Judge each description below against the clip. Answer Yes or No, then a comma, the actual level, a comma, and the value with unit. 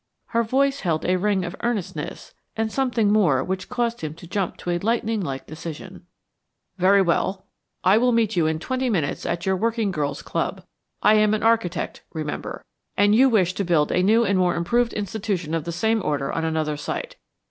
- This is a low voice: No, high, 195 Hz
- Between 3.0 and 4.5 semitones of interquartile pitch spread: No, average, 4.9 semitones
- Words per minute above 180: Yes, average, 195 wpm